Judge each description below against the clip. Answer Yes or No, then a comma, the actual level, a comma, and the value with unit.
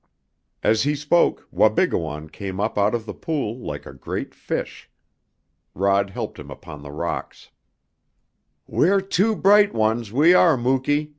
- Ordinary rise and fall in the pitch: No, wide, 7.7 semitones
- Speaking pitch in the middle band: No, low, 120 Hz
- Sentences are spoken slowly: No, average, 145 wpm